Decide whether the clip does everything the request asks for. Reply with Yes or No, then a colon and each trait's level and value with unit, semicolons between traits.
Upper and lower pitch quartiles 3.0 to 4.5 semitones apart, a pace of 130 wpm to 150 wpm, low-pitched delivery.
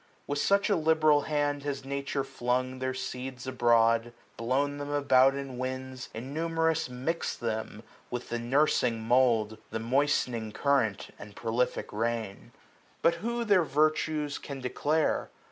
Yes: average, 3.6 semitones; average, 140 wpm; low, 130 Hz